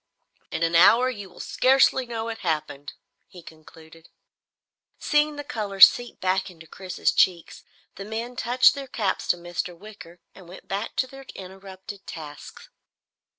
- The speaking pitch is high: Yes, high, 195 Hz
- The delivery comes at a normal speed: Yes, average, 150 wpm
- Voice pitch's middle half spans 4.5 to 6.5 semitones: Yes, wide, 5.5 semitones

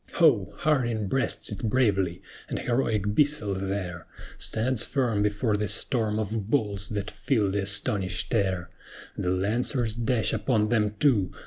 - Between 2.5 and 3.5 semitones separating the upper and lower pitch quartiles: Yes, average, 3.2 semitones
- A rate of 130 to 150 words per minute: Yes, average, 140 wpm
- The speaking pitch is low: Yes, low, 105 Hz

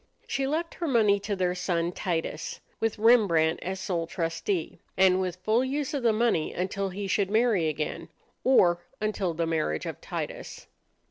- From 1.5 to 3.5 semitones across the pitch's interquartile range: No, average, 4.9 semitones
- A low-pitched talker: No, high, 190 Hz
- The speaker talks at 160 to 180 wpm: Yes, average, 165 wpm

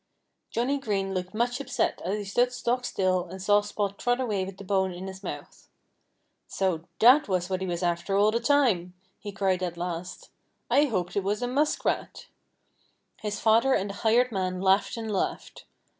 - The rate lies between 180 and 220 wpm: Yes, average, 190 wpm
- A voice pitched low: No, high, 200 Hz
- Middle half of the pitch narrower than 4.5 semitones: Yes, average, 4.0 semitones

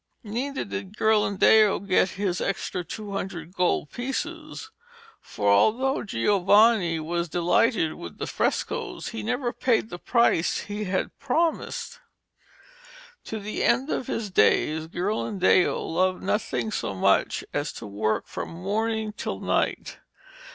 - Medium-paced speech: No, slow, 130 wpm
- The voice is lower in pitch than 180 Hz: No, high, 200 Hz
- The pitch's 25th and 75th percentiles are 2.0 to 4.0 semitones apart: No, average, 4.6 semitones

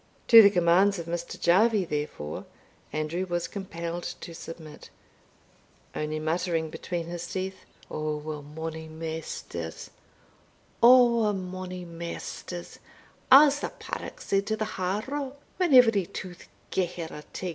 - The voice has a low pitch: No, medium, 175 Hz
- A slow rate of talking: Yes, slow, 125 wpm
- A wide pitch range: No, average, 3.8 semitones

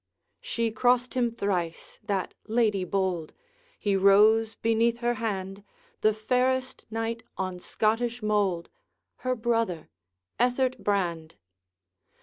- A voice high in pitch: Yes, high, 220 Hz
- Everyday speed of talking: No, slow, 110 wpm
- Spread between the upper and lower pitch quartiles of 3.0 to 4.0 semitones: Yes, average, 3.4 semitones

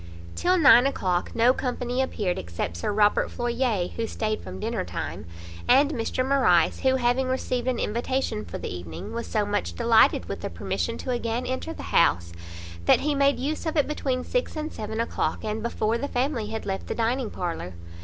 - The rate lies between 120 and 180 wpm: No, average, 195 wpm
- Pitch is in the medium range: No, high, 235 Hz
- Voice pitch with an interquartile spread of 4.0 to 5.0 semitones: Yes, average, 4.3 semitones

